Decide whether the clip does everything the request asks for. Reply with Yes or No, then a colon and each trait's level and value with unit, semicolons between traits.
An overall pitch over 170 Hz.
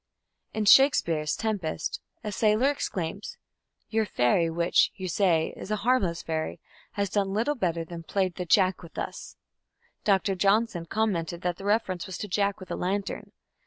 Yes: high, 190 Hz